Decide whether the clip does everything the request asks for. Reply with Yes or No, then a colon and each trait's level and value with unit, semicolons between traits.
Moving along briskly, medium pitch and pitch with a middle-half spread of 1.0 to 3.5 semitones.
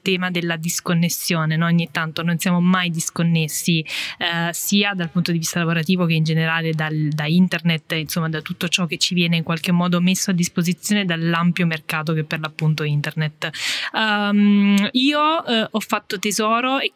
Yes: fast, 175 wpm; medium, 175 Hz; narrow, 2.4 semitones